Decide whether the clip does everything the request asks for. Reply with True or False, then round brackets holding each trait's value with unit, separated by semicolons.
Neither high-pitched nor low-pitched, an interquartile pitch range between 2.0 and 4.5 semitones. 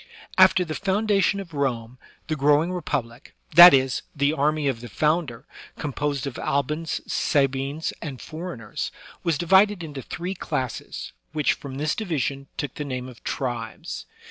True (145 Hz; 4.1 semitones)